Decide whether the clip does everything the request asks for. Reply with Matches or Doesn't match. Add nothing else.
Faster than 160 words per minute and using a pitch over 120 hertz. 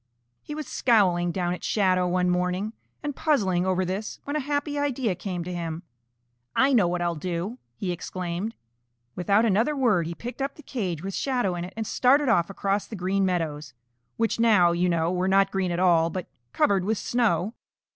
Matches